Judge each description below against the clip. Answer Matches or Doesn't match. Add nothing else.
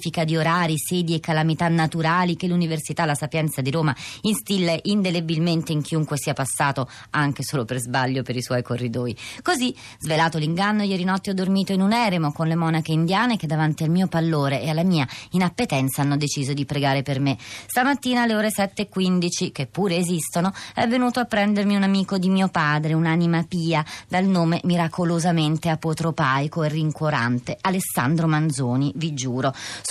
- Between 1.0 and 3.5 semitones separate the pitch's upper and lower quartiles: Doesn't match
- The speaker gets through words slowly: Doesn't match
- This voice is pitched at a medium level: Matches